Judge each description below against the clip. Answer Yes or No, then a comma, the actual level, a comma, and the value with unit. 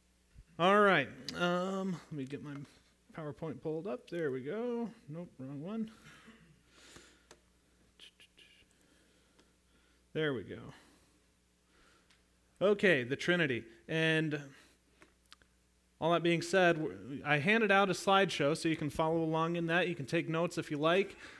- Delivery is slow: Yes, slow, 130 wpm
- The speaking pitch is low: No, medium, 155 Hz